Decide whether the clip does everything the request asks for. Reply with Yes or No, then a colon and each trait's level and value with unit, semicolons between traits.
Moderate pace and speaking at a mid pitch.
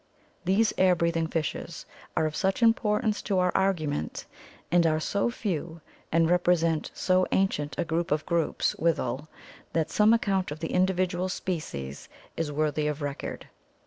Yes: average, 150 wpm; medium, 170 Hz